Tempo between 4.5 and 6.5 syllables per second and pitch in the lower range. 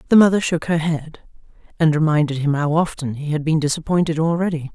No: 6.0 syllables/s; medium, 155 Hz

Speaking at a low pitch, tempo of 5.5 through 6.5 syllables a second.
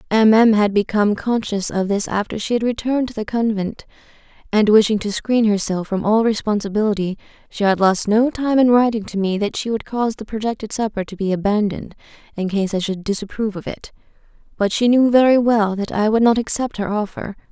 No: high, 215 Hz; 5.8 syllables/s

